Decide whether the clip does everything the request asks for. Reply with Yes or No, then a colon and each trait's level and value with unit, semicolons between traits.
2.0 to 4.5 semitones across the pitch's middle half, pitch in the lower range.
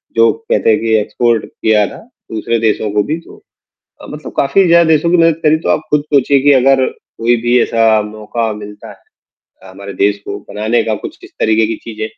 No: average, 5.0 semitones; low, 115 Hz